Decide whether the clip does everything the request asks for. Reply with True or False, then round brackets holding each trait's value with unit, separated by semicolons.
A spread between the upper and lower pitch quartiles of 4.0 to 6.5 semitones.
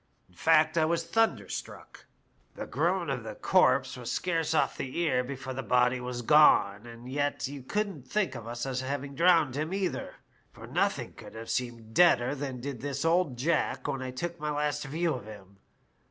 True (4.6 semitones)